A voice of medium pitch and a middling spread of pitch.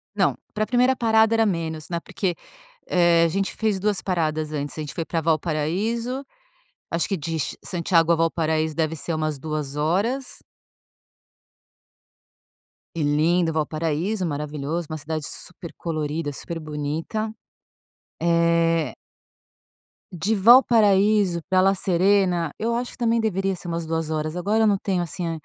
Yes: medium, 170 Hz; average, 4.1 semitones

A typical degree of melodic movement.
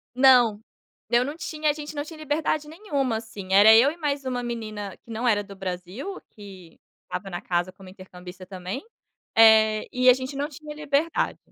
No: wide, 6.6 semitones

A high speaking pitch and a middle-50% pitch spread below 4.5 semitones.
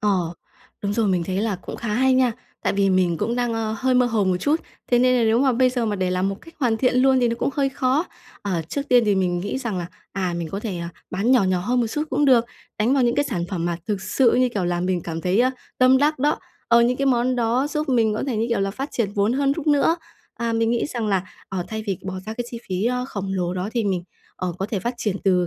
No: high, 225 Hz; average, 4.9 semitones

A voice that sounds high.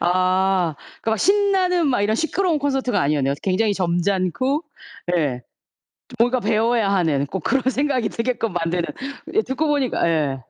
Yes: high, 215 Hz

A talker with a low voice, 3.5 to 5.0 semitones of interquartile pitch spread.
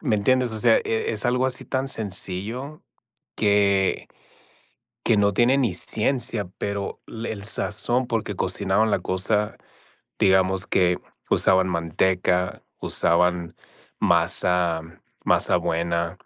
Yes: low, 100 Hz; average, 3.8 semitones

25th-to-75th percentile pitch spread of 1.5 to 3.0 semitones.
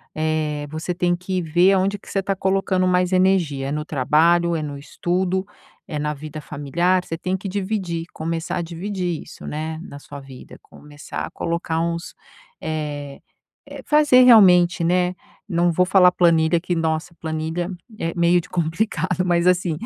Yes: narrow, 2.6 semitones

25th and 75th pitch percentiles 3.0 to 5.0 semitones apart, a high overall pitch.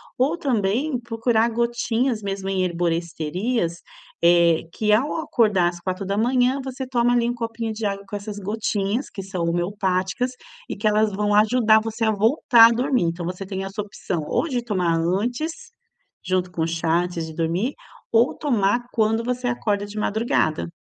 Yes: average, 4.4 semitones; high, 210 Hz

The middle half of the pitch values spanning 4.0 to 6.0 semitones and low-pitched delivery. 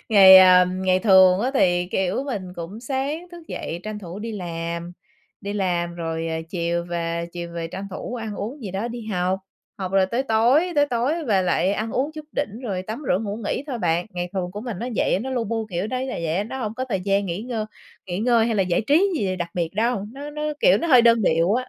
No: average, 5.0 semitones; high, 200 Hz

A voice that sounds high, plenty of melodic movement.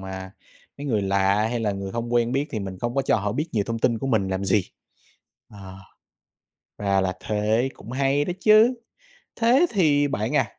No: low, 115 Hz; wide, 5.9 semitones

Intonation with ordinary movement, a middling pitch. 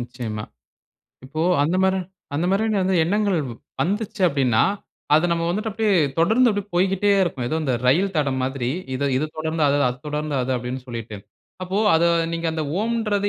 No: wide, 6.9 semitones; medium, 165 Hz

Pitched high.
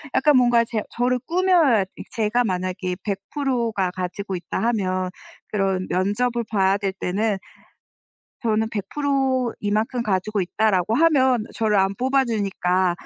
Yes: high, 215 Hz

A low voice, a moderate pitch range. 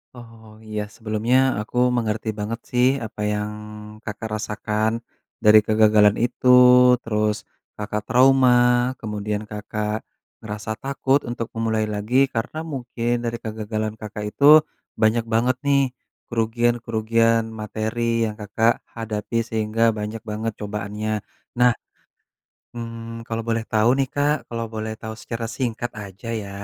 No: low, 110 Hz; narrow, 1.5 semitones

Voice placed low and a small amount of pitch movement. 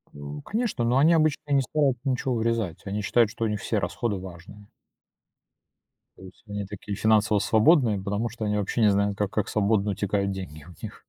No: low, 105 Hz; average, 3.2 semitones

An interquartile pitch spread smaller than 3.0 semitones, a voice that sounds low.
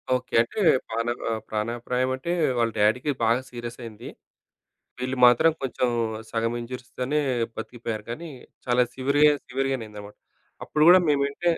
Yes: narrow, 2.6 semitones; low, 125 Hz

